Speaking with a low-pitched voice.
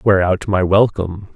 Yes: very low, 95 Hz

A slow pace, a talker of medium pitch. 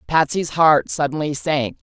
Yes: slow, 125 wpm; medium, 150 Hz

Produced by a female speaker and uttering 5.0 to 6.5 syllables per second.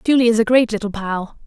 Yes: female; 6.2 syllables/s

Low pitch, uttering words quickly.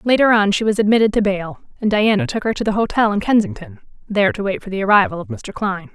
No: high, 205 Hz; fast, 250 wpm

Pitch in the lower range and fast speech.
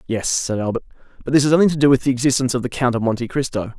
Yes: low, 125 Hz; fast, 285 wpm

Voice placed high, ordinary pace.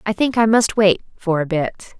No: high, 200 Hz; fast, 240 wpm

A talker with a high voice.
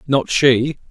No: low, 135 Hz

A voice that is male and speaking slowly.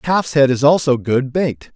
No: male; fast, 205 wpm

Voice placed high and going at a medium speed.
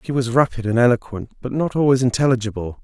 No: low, 125 Hz; average, 190 wpm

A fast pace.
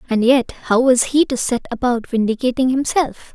No: average, 180 wpm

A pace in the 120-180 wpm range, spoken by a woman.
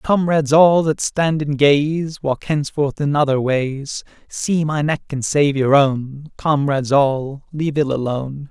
No: average, 160 wpm; male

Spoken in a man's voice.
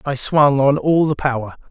Yes: male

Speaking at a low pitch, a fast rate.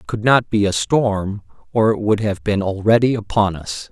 Yes: low, 105 Hz; fast, 215 wpm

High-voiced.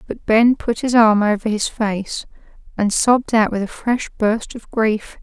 Yes: high, 220 Hz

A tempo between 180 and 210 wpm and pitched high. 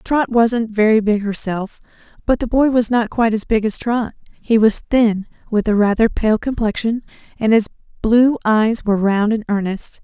Yes: average, 185 wpm; high, 220 Hz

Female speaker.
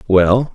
No: male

